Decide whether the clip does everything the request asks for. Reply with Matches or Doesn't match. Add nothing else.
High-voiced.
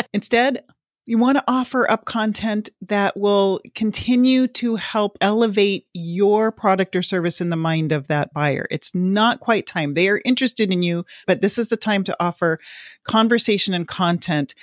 Matches